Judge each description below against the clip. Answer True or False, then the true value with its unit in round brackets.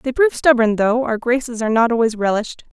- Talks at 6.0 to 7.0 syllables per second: True (6.4 syllables/s)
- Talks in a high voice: True (235 Hz)